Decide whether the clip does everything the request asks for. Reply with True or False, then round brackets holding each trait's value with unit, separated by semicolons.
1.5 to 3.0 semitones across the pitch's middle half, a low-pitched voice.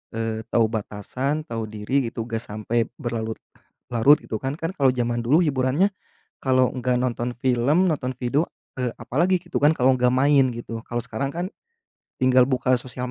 True (2.7 semitones; 125 Hz)